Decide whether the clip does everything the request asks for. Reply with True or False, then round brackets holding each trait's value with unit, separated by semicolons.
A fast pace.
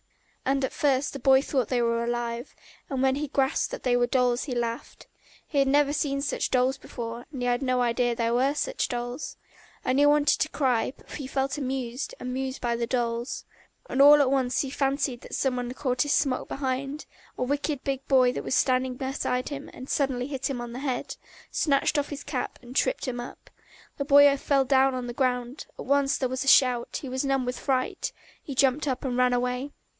True (215 wpm)